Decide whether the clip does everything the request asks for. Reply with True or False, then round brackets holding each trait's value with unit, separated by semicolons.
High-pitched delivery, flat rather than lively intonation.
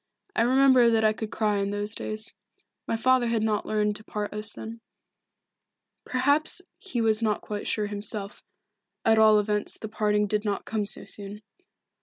True (215 Hz; 1.6 semitones)